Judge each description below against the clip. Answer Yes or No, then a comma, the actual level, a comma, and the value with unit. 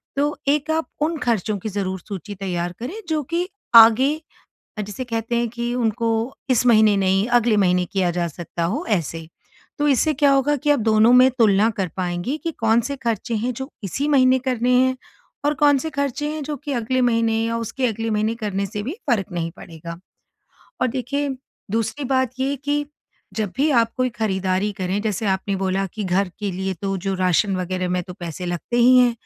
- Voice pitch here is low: No, high, 225 Hz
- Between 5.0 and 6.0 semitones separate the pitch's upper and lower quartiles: Yes, average, 5.3 semitones